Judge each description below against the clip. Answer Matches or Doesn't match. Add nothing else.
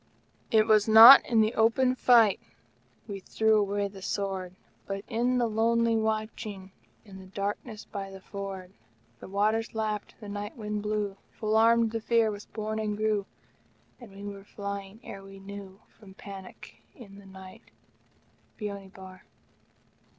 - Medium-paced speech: Matches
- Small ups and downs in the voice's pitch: Matches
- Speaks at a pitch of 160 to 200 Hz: Doesn't match